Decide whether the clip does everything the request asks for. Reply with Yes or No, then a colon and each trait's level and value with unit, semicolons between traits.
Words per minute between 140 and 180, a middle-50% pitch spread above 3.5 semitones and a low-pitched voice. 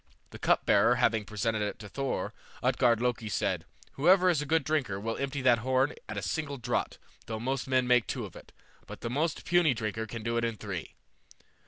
No: fast, 205 wpm; average, 3.9 semitones; low, 120 Hz